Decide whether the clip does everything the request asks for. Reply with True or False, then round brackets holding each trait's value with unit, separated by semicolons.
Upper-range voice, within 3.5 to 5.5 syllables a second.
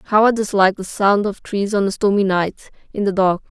True (200 Hz; 5.3 syllables/s)